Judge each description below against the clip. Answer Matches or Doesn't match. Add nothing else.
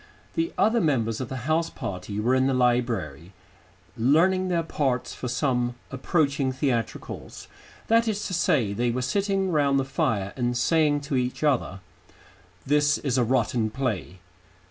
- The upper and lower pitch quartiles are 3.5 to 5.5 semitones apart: Matches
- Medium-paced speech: Matches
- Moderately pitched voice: Doesn't match